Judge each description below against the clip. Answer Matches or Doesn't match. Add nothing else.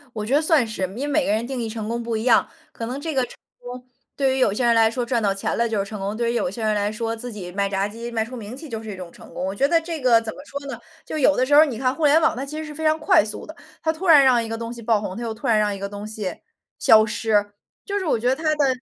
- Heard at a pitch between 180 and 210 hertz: Doesn't match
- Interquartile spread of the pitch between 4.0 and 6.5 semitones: Matches